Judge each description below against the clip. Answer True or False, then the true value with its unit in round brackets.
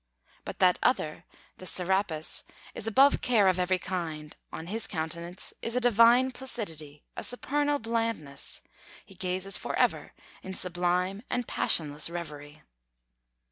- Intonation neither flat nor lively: False (5.8 semitones)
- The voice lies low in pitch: False (185 Hz)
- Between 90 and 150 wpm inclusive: True (135 wpm)